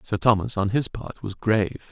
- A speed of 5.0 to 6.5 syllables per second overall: Yes, 5.4 syllables/s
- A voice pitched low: Yes, low, 105 Hz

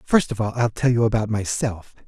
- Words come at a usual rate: No, fast, 230 wpm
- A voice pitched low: Yes, low, 115 Hz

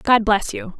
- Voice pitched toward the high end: Yes, high, 235 Hz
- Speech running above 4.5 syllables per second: No, 4.0 syllables/s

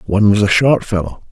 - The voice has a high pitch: No, low, 105 Hz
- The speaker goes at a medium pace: No, fast, 225 wpm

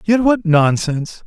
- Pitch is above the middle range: No, medium, 180 Hz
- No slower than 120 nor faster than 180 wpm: Yes, average, 140 wpm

